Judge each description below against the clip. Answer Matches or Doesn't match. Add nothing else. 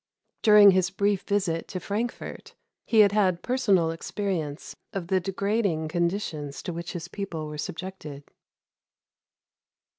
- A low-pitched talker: Doesn't match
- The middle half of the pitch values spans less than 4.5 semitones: Matches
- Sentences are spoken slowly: Matches